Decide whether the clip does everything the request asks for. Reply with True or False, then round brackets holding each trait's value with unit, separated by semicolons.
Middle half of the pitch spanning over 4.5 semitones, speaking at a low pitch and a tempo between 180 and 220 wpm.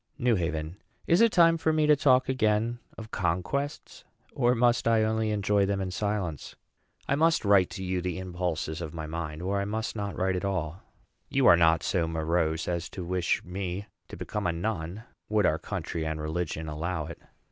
True (4.9 semitones; 95 Hz; 195 wpm)